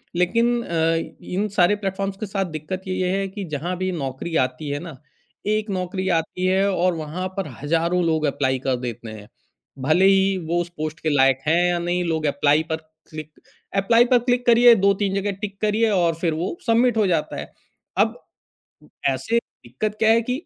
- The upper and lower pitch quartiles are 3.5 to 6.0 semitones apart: Yes, average, 4.2 semitones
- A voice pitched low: No, medium, 180 Hz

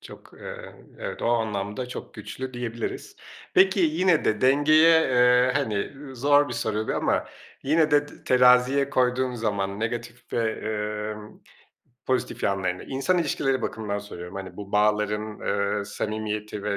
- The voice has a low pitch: Yes, low, 120 Hz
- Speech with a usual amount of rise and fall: Yes, average, 4.5 semitones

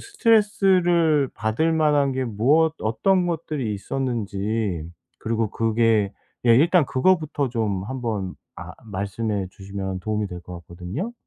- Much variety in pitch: Yes, wide, 7.6 semitones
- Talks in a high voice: No, low, 115 Hz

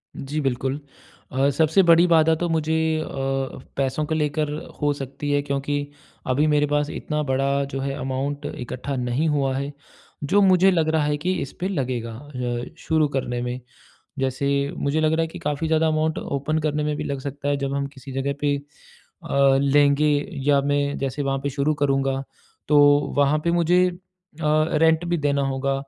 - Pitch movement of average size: No, narrow, 2.2 semitones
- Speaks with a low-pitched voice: No, medium, 145 Hz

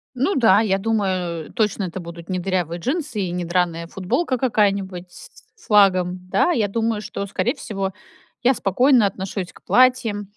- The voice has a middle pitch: No, high, 195 Hz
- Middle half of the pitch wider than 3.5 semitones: Yes, average, 3.9 semitones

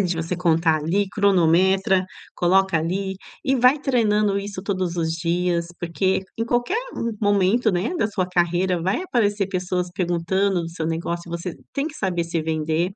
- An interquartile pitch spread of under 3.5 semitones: Yes, average, 3.0 semitones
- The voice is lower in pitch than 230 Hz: Yes, medium, 185 Hz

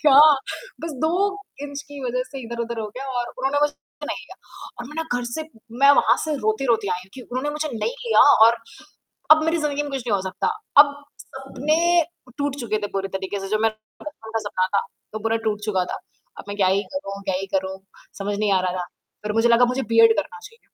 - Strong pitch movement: Yes, wide, 5.7 semitones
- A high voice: Yes, high, 235 Hz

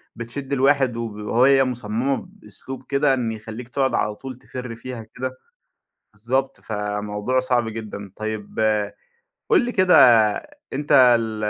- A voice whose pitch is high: No, low, 125 Hz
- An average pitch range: Yes, average, 3.4 semitones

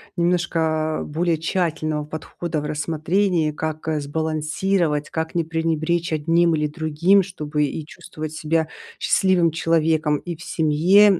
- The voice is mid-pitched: Yes, medium, 160 Hz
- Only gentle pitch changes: Yes, narrow, 1.8 semitones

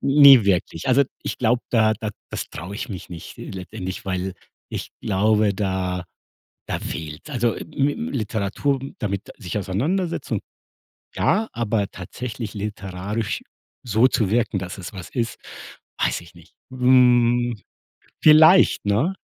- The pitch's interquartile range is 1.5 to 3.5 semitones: No, average, 4.7 semitones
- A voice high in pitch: No, low, 110 Hz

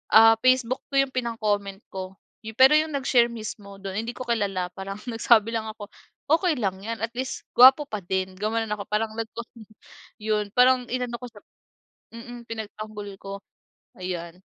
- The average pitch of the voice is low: No, high, 225 Hz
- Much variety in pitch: No, average, 3.2 semitones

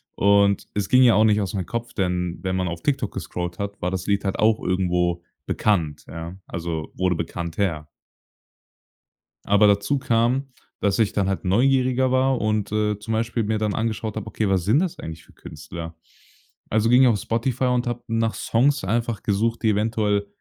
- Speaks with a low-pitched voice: Yes, low, 105 Hz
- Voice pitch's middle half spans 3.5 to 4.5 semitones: Yes, average, 3.8 semitones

